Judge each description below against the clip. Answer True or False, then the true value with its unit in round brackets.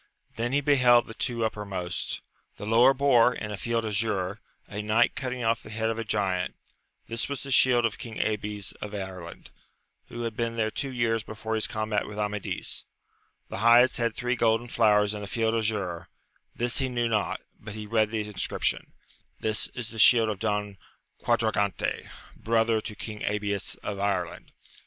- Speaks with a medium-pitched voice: False (110 Hz)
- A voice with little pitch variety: True (2.1 semitones)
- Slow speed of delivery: False (180 wpm)